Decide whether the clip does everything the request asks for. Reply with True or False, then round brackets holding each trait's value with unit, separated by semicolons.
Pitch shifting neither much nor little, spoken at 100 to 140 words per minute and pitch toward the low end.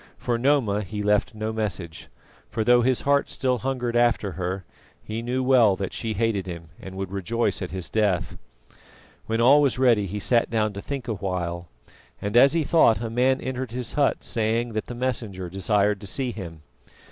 False (4.0 semitones; 195 wpm; 110 Hz)